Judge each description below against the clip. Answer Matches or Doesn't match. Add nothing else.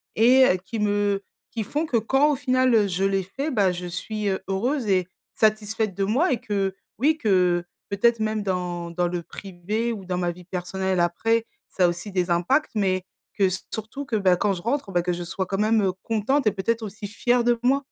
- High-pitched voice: Matches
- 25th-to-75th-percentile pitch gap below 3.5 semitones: Doesn't match